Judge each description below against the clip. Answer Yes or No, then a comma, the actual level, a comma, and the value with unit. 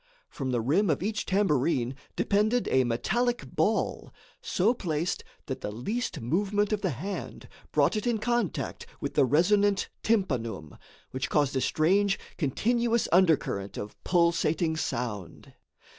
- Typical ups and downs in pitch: No, wide, 7.9 semitones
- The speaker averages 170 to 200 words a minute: No, slow, 135 wpm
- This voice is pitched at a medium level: Yes, medium, 170 Hz